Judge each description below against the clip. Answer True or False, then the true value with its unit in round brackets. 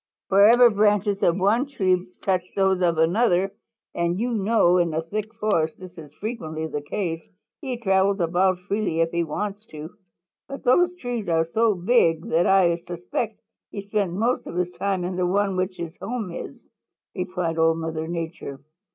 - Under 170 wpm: False (175 wpm)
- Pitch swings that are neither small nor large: True (3.8 semitones)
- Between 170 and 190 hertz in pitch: True (185 Hz)